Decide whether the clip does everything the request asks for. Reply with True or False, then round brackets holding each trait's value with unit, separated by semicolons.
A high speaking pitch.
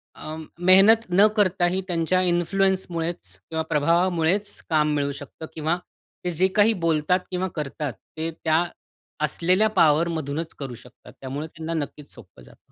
False (165 Hz)